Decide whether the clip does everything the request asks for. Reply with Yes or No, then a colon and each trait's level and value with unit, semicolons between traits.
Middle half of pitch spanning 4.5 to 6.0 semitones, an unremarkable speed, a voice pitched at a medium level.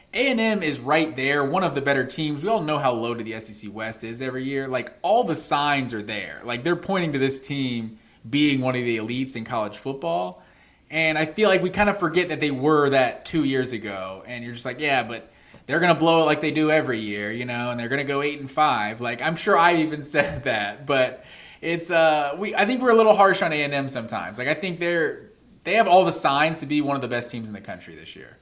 No: average, 5.3 semitones; fast, 255 wpm; medium, 145 Hz